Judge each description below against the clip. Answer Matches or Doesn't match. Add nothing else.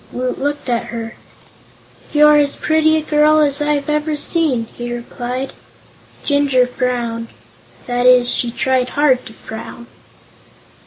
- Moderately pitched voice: Doesn't match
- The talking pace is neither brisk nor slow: Doesn't match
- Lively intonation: Doesn't match